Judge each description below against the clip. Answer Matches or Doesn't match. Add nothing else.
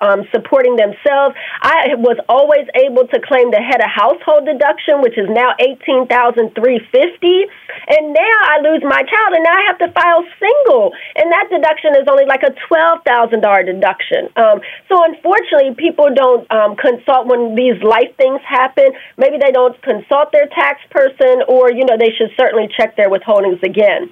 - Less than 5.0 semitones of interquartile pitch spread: Doesn't match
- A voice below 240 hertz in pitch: Doesn't match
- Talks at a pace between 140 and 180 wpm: Matches